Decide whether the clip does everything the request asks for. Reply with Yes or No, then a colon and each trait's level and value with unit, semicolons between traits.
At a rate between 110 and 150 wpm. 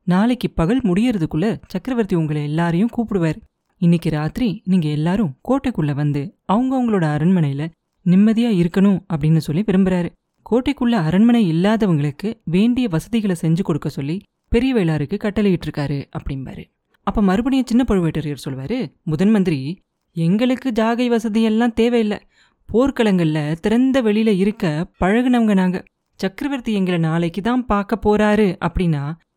Yes: average, 115 wpm